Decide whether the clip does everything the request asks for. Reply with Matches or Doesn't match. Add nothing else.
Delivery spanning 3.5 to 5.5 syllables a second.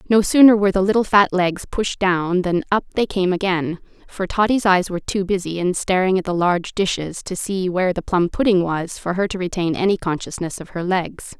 Matches